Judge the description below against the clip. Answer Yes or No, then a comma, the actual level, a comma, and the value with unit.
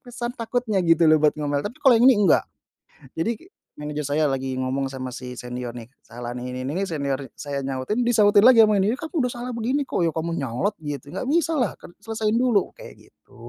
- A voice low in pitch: No, medium, 165 Hz